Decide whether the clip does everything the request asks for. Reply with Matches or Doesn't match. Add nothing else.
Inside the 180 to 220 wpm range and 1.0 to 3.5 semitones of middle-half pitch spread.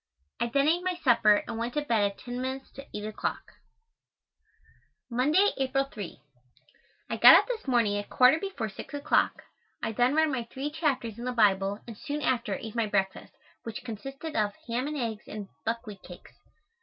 Doesn't match